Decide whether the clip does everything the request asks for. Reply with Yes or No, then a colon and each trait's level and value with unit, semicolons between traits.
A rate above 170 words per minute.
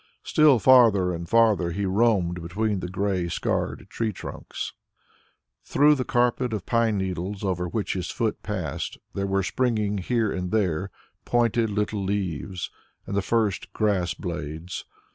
No: average, 145 wpm